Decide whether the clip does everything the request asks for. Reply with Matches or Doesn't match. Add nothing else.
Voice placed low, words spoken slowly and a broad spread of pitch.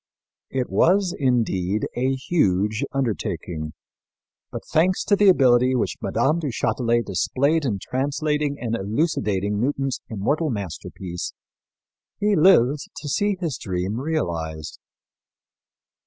Matches